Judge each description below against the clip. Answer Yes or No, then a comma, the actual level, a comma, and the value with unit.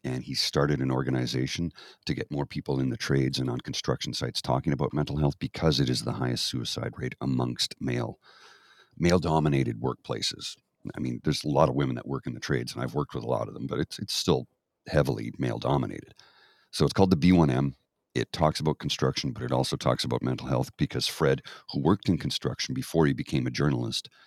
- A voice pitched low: Yes, very low, 65 Hz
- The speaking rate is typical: No, fast, 215 wpm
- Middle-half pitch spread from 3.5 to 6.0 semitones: No, narrow, 2.4 semitones